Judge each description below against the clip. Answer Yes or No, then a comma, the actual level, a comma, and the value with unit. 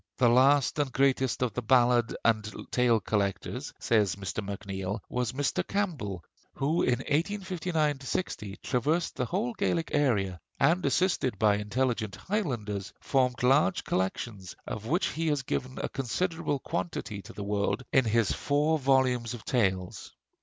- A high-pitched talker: No, low, 125 Hz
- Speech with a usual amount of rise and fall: No, wide, 5.7 semitones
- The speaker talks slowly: No, average, 145 wpm